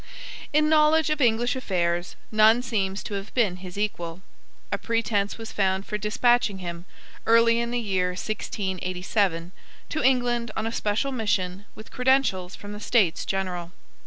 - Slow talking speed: No, average, 155 wpm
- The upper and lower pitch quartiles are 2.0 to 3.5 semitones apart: No, average, 4.2 semitones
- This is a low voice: No, high, 210 Hz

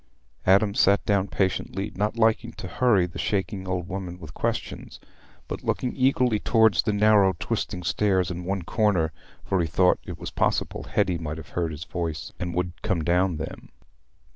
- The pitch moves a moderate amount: Yes, average, 3.1 semitones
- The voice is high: No, very low, 95 Hz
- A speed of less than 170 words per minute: No, average, 175 wpm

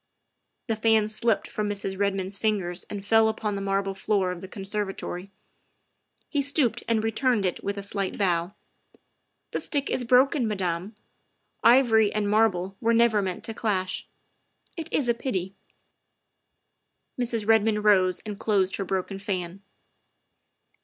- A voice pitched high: Yes, high, 205 Hz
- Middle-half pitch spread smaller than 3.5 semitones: Yes, narrow, 2.6 semitones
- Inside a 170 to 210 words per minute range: No, average, 160 wpm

